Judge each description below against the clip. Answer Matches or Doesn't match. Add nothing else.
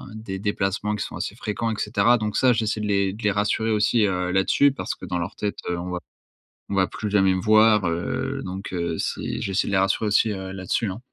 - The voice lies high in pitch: Doesn't match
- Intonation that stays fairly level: Matches